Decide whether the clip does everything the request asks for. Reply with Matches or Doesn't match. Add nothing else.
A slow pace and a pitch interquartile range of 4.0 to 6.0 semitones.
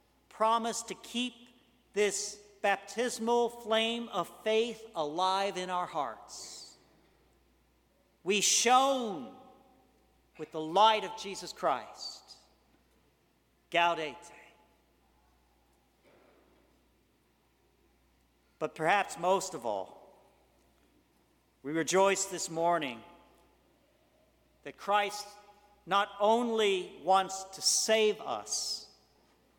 Matches